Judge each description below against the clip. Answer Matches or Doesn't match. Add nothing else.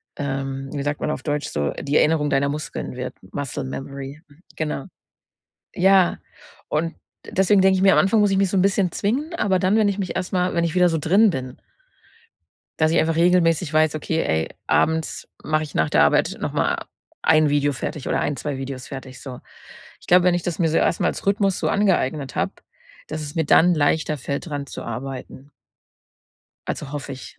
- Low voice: Doesn't match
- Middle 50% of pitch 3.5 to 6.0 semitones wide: Matches